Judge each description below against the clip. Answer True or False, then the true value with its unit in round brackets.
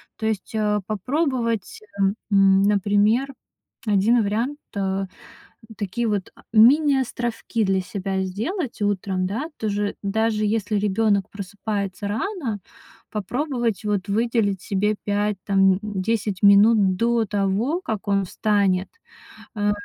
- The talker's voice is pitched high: True (210 Hz)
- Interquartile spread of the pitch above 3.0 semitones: False (2.5 semitones)